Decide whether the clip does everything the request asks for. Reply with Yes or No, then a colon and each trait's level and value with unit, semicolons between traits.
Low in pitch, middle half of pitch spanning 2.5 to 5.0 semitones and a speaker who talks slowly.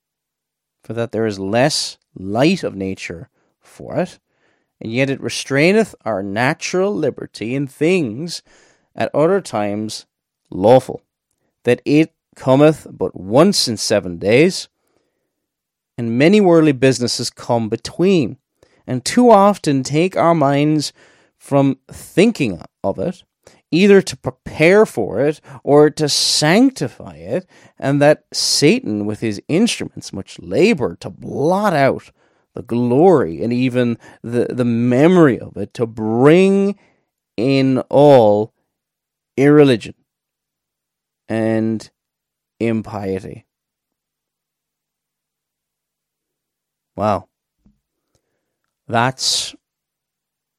No: low, 130 Hz; wide, 5.6 semitones; slow, 100 wpm